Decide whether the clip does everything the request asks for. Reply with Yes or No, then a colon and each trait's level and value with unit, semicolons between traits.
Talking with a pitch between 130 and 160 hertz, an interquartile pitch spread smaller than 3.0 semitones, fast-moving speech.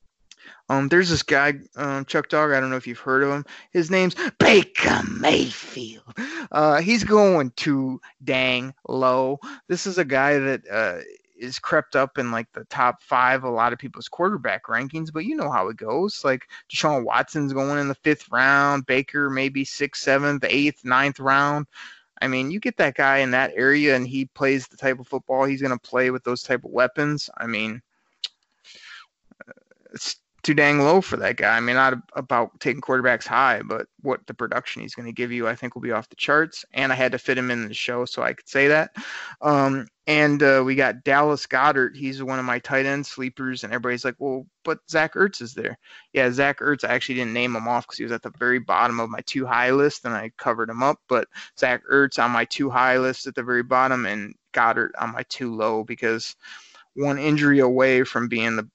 Yes: low, 135 Hz; narrow, 2.4 semitones; fast, 215 wpm